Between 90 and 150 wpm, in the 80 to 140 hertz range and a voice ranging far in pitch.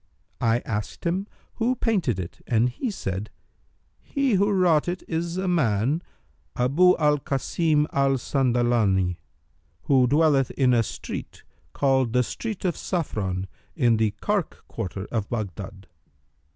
Yes: average, 140 wpm; low, 135 Hz; wide, 7.5 semitones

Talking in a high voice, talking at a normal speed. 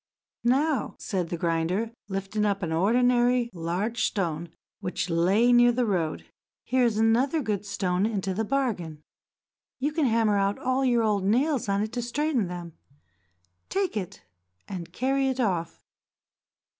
Yes: high, 215 Hz; average, 155 wpm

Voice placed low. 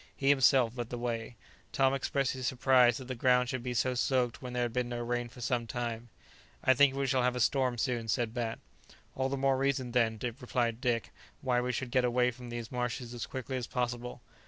Yes: low, 125 Hz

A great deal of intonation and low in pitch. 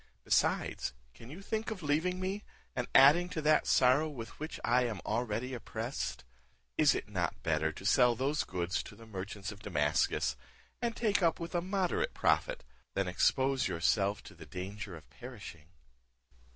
Yes: wide, 8.8 semitones; low, 125 Hz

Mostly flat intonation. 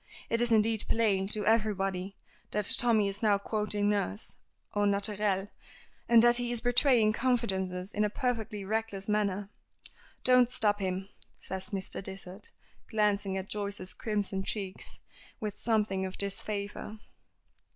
Yes: narrow, 2.3 semitones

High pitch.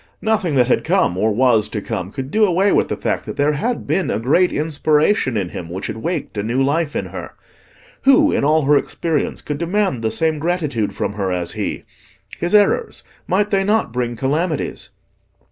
No: medium, 150 Hz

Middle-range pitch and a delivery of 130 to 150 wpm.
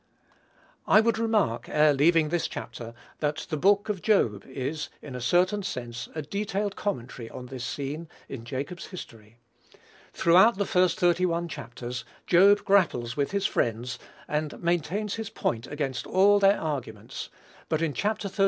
No: medium, 160 Hz; average, 160 wpm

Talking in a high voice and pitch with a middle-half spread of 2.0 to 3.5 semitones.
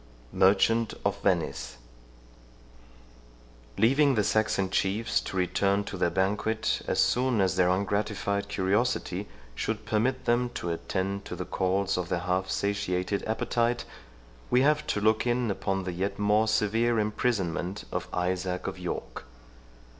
No: low, 100 Hz; average, 3.0 semitones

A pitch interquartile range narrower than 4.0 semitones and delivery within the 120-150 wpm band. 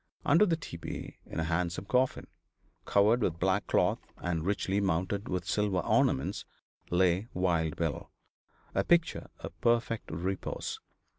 Yes: average, 3.5 semitones; slow, 135 wpm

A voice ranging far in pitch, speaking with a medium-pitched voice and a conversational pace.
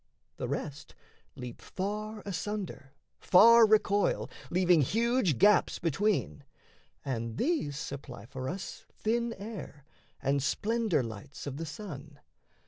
No: wide, 7.3 semitones; medium, 170 Hz; slow, 115 wpm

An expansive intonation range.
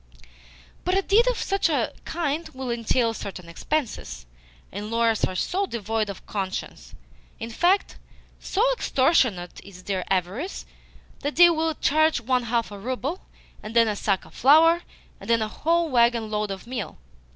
Yes: wide, 7.2 semitones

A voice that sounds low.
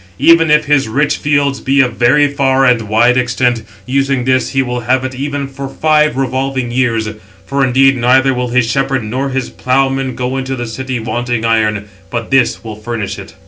Yes: low, 130 Hz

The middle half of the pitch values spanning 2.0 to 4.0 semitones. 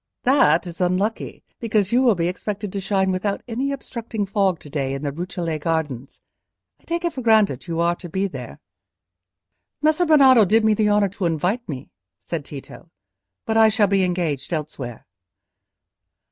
No: average, 5.0 semitones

